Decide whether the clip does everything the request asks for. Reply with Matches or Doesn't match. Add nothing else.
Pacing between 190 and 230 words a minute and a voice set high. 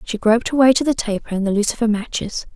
Doesn't match